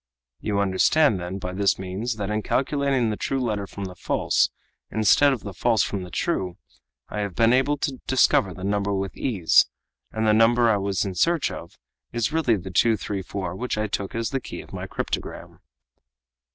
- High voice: No, low, 105 Hz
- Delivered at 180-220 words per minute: Yes, average, 190 wpm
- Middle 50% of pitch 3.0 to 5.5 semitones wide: Yes, average, 3.9 semitones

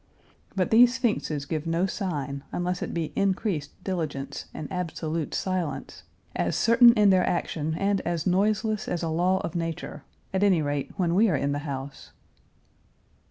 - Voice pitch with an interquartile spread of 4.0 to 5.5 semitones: Yes, average, 4.4 semitones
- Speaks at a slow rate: No, average, 160 wpm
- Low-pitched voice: No, medium, 175 Hz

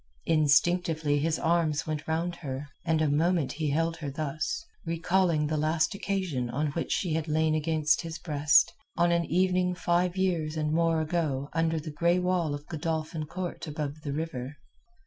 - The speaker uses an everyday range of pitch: No, narrow, 2.3 semitones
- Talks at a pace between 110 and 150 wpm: No, average, 170 wpm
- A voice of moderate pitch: Yes, medium, 160 Hz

